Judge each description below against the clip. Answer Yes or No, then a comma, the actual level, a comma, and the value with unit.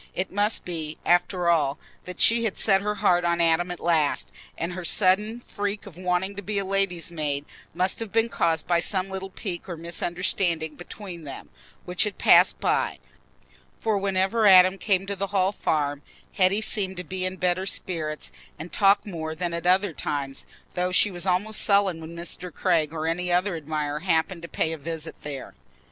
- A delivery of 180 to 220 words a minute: Yes, average, 190 wpm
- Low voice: No, medium, 180 Hz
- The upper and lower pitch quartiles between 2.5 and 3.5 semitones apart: Yes, average, 2.9 semitones